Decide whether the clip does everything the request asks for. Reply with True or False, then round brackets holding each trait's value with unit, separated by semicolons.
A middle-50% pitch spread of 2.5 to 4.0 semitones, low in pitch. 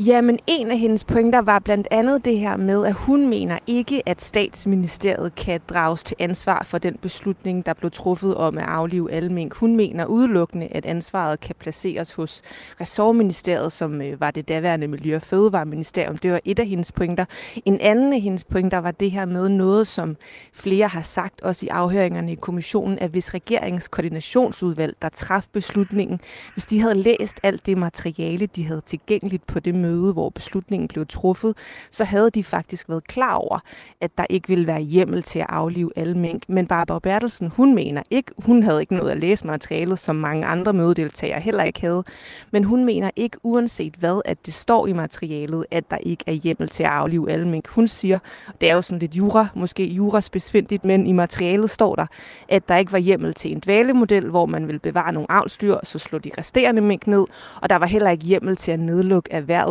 False (3.5 semitones; 185 Hz)